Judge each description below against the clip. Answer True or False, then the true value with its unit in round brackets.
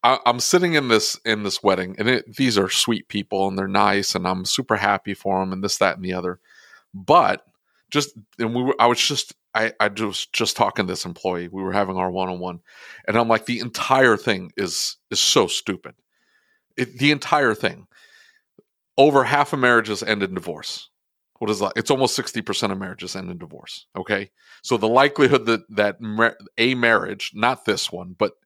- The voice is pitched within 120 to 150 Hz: False (110 Hz)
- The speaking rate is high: False (195 wpm)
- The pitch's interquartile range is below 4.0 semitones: False (4.3 semitones)